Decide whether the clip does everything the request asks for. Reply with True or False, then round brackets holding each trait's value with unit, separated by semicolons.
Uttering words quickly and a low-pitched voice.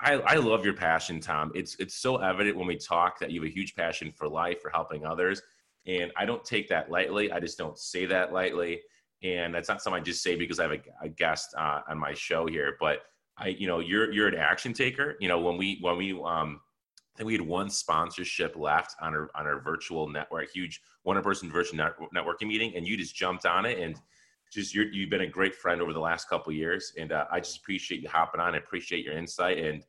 True (250 wpm; 90 Hz)